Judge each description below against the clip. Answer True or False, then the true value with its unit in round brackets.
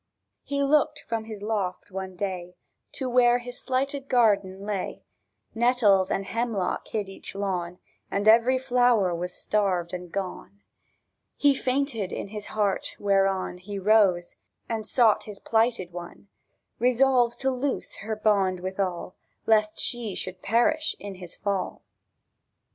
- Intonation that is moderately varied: True (4.2 semitones)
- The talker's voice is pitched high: True (210 Hz)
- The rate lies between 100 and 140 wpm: True (135 wpm)